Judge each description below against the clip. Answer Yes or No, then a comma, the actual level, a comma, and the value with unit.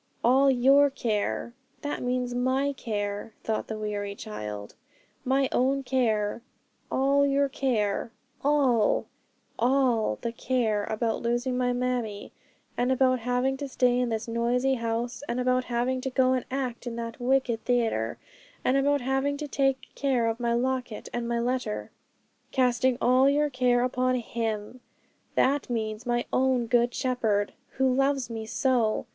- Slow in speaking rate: No, average, 150 wpm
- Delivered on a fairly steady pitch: Yes, narrow, 2.2 semitones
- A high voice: Yes, very high, 250 Hz